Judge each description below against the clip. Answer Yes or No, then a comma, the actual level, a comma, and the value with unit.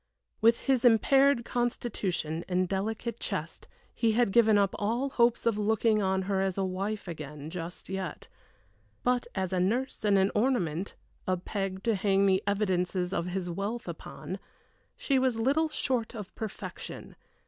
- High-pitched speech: Yes, high, 205 Hz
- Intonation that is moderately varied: Yes, average, 3.9 semitones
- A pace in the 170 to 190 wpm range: No, average, 160 wpm